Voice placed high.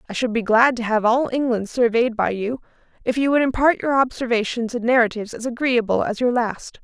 Yes: high, 240 Hz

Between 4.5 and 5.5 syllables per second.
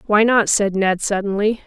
Yes: 4.8 syllables/s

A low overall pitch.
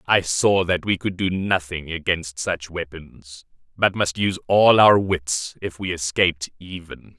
Yes: very low, 90 Hz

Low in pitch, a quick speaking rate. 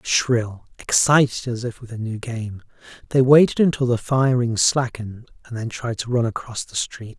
No: low, 120 Hz; average, 185 wpm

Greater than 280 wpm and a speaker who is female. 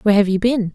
Yes: fast, 320 wpm; female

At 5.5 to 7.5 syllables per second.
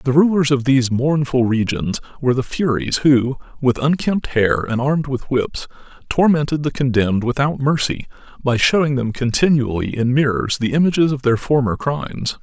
No: 5.1 syllables/s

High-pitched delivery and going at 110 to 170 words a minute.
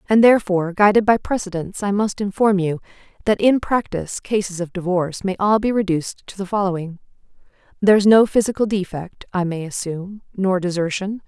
Yes: high, 195 Hz; average, 160 wpm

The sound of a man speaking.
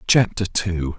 Yes: male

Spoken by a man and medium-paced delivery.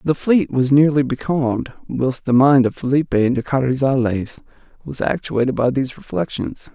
Yes: male; average, 150 wpm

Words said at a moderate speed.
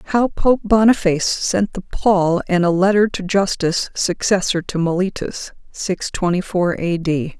Yes: average, 155 wpm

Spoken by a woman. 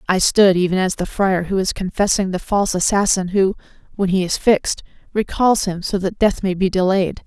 Yes: female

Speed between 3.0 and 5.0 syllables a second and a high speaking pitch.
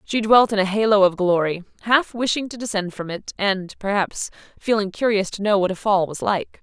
No: 5.2 syllables/s; high, 205 Hz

